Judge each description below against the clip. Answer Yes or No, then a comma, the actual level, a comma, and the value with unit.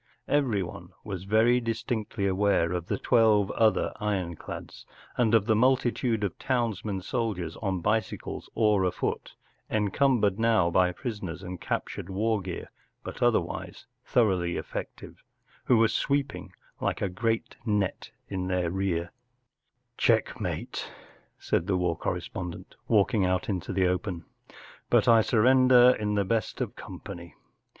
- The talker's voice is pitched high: No, low, 105 Hz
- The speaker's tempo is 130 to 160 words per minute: Yes, average, 145 wpm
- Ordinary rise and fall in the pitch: Yes, average, 3.9 semitones